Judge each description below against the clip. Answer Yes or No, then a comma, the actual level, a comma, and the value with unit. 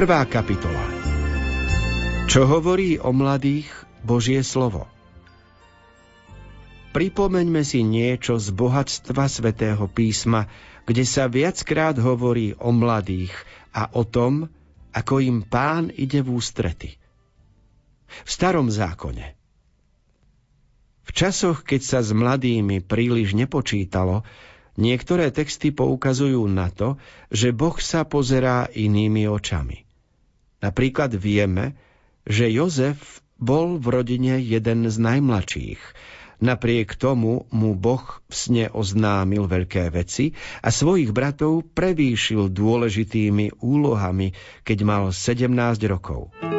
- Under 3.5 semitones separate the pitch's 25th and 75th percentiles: No, average, 4.6 semitones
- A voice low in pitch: Yes, low, 115 Hz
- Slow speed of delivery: Yes, slow, 105 wpm